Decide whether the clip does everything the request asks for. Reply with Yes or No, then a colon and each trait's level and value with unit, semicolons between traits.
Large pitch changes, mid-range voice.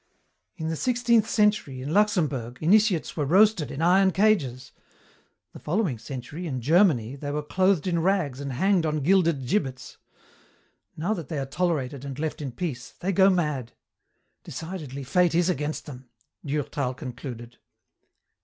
Yes: wide, 5.7 semitones; medium, 155 Hz